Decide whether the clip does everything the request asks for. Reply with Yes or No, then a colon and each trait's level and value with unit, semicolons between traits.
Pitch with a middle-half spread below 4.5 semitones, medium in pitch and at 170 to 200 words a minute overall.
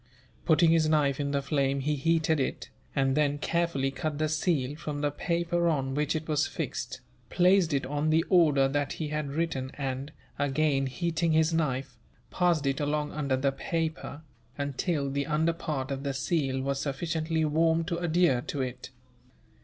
Yes: average, 2.8 semitones; medium, 150 Hz; average, 175 wpm